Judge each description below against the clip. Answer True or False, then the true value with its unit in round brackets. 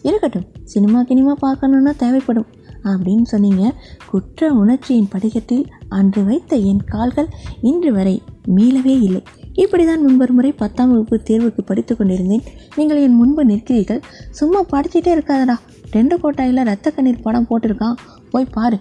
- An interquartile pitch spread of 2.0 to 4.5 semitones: True (4.2 semitones)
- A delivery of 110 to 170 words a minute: True (130 wpm)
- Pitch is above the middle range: True (245 Hz)